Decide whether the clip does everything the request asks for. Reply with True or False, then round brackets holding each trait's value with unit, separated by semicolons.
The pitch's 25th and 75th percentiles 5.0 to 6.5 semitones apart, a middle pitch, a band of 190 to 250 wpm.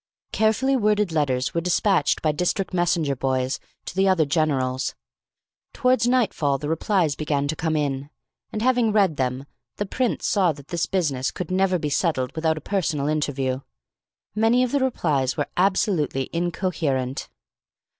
False (5.6 semitones; 165 Hz; 155 wpm)